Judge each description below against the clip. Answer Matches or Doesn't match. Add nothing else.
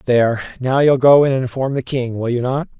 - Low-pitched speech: Matches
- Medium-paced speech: Doesn't match